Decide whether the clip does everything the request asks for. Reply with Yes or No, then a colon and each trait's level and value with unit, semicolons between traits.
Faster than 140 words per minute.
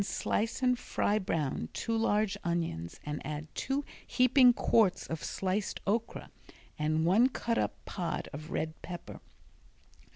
No: slow, 135 wpm